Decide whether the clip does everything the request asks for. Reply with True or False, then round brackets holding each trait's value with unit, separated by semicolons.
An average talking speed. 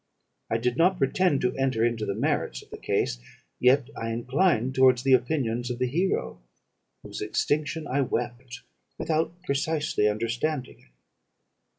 True (150 wpm)